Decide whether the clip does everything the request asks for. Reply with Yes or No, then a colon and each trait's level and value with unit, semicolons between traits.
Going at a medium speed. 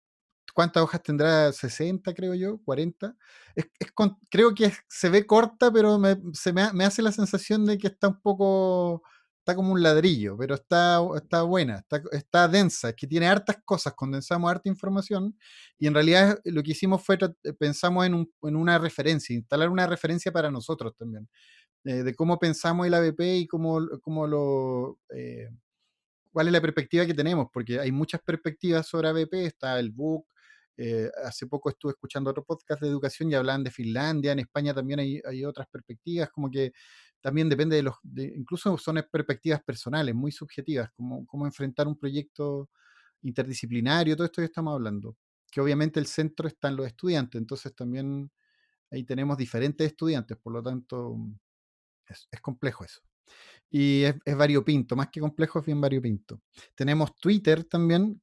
Yes: average, 175 wpm